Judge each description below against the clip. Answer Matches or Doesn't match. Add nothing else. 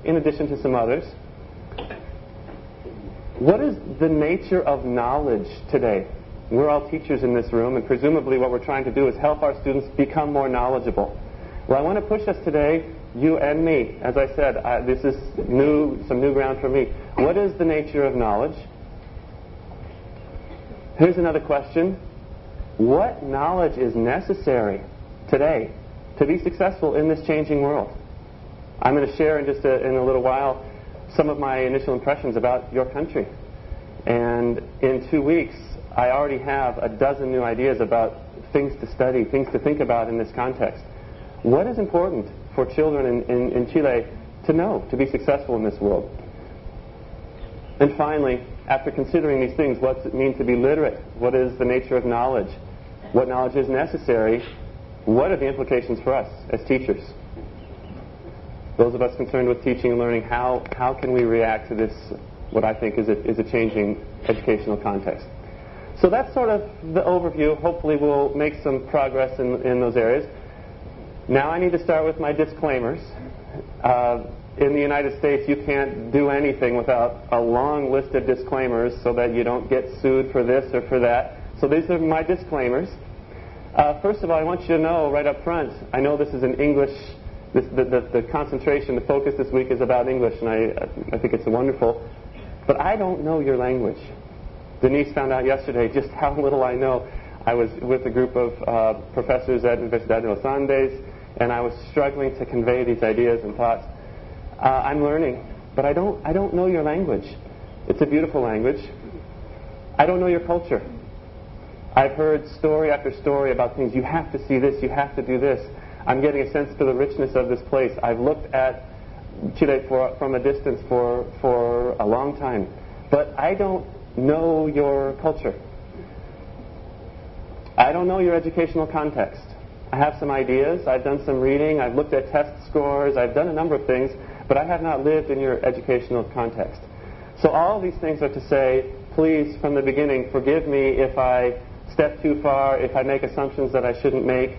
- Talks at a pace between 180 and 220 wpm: Matches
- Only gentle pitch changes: Doesn't match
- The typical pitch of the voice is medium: Doesn't match